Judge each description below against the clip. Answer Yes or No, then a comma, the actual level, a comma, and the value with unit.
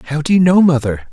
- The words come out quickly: Yes, fast, 270 wpm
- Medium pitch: Yes, medium, 150 Hz